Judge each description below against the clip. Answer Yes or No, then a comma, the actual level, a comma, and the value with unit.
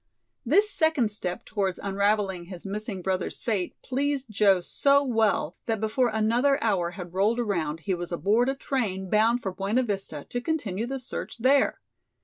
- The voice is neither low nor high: No, high, 215 Hz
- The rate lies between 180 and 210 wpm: No, average, 165 wpm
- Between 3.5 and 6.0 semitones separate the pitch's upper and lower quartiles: Yes, average, 4.5 semitones